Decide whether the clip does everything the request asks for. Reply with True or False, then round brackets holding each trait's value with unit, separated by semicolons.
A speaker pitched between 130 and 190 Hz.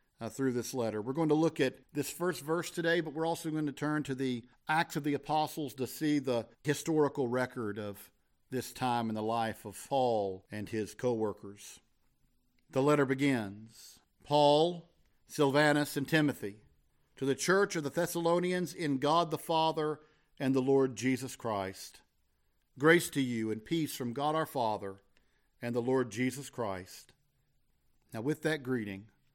True (135 Hz)